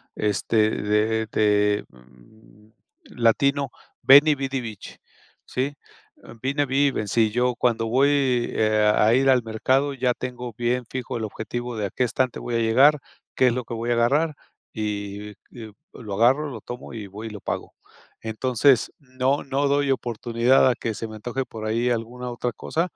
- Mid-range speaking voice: No, low, 120 Hz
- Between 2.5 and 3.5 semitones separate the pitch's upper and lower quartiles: Yes, average, 3.2 semitones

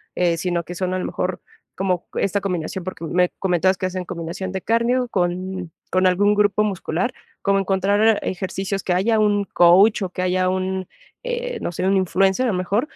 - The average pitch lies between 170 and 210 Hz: Yes, high, 190 Hz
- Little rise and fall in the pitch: Yes, narrow, 2.0 semitones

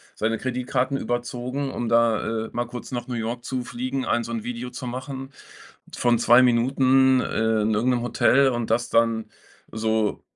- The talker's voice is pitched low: Yes, low, 120 Hz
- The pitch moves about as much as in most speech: No, narrow, 2.0 semitones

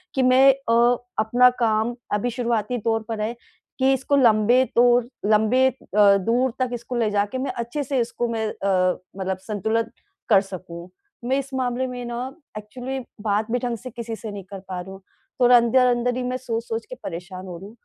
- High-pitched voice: Yes, high, 235 Hz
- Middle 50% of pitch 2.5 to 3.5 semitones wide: Yes, average, 3.2 semitones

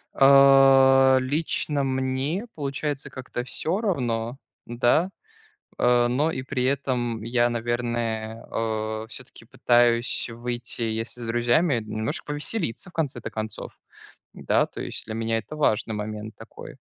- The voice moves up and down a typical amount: Yes, average, 3.2 semitones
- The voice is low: Yes, low, 120 Hz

